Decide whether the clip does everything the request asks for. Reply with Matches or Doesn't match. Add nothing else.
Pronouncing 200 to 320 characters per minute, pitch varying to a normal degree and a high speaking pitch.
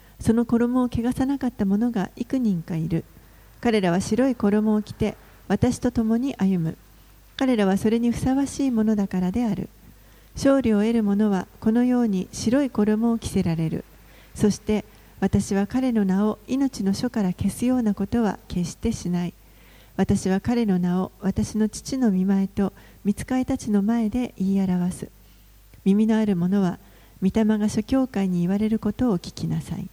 Matches